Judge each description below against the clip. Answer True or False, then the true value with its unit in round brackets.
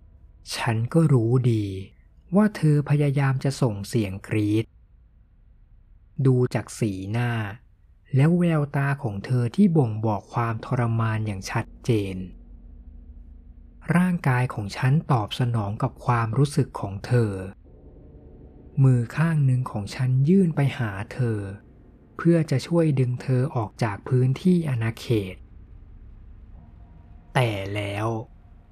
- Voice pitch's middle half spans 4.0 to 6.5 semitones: True (5.5 semitones)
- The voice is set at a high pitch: False (115 Hz)